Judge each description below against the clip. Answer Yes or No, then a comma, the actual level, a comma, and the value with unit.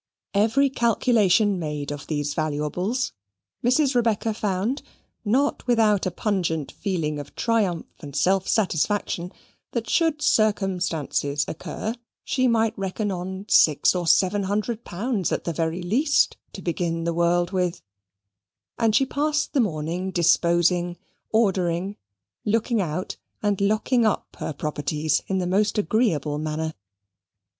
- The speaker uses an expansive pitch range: No, average, 4.9 semitones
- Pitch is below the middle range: No, high, 190 Hz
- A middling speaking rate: No, slow, 130 wpm